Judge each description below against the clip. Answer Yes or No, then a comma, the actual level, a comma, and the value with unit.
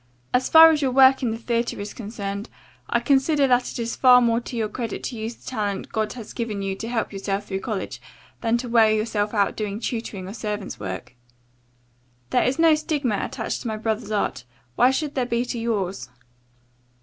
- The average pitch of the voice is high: Yes, high, 230 Hz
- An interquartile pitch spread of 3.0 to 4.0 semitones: Yes, average, 3.3 semitones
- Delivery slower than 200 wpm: No, fast, 205 wpm